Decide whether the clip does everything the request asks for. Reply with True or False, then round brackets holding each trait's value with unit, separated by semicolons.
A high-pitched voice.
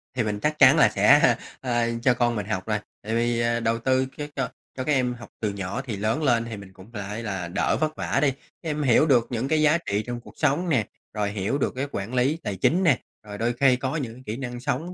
False (120 Hz)